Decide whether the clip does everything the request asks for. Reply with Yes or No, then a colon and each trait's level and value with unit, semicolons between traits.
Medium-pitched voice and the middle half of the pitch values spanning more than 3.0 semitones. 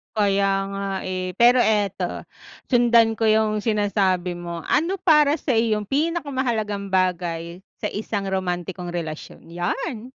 No: high, 205 Hz; average, 4.3 semitones